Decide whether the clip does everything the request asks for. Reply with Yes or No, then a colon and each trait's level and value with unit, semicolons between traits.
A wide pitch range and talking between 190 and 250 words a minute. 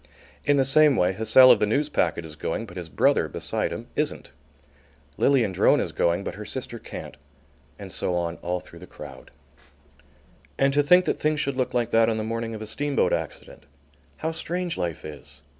Yes: wide, 7.5 semitones; average, 195 wpm